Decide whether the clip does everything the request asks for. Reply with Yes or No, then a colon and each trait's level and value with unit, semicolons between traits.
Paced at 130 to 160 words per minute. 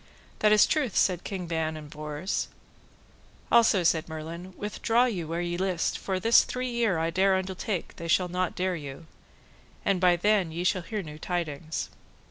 No: average, 175 wpm